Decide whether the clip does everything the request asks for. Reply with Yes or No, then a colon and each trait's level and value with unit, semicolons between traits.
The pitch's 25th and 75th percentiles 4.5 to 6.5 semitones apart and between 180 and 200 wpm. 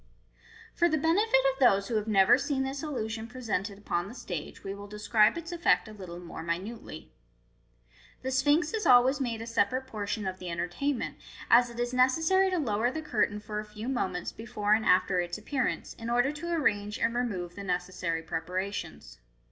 Yes: average, 5.2 semitones; average, 190 wpm